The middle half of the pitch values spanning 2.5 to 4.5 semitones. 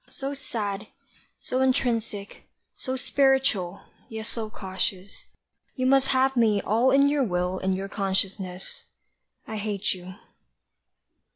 No: average, 5.2 semitones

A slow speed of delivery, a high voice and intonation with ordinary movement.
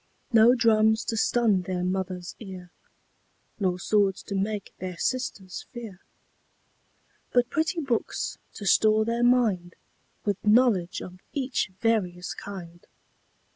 Yes: slow, 120 wpm; high, 210 Hz; average, 4.1 semitones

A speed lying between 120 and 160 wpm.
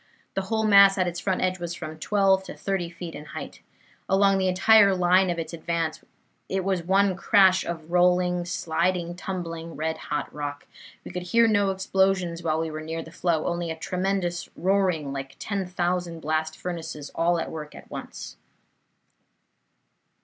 No: average, 170 wpm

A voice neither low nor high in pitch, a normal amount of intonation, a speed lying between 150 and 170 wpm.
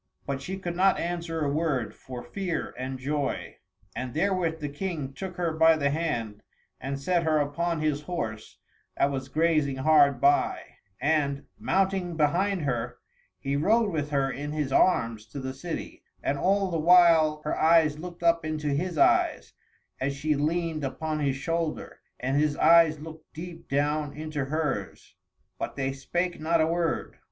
Yes: medium, 155 Hz; average, 3.3 semitones; average, 165 wpm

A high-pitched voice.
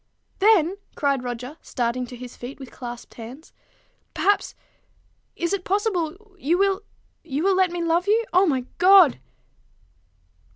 Yes: very high, 335 Hz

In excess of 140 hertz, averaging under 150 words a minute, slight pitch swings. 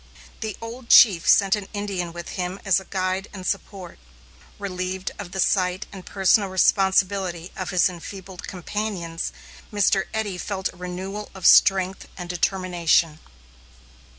Yes: high, 190 Hz; average, 140 wpm; narrow, 1.8 semitones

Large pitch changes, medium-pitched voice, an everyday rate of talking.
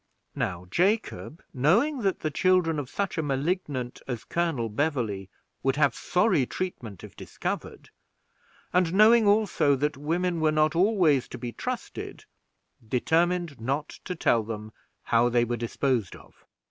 Yes: wide, 6.7 semitones; medium, 150 Hz; average, 145 wpm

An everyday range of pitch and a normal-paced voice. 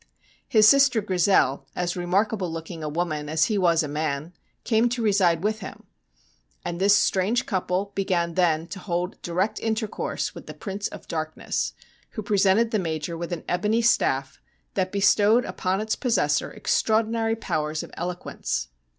Yes: average, 4.4 semitones; average, 160 wpm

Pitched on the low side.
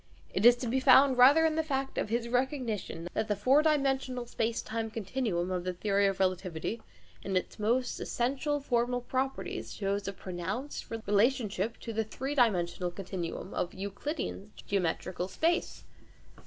No: high, 225 Hz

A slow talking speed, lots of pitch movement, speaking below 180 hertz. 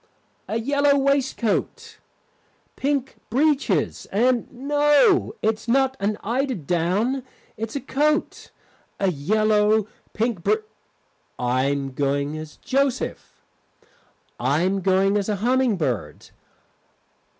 No: slow, 105 wpm; wide, 7.0 semitones; high, 220 Hz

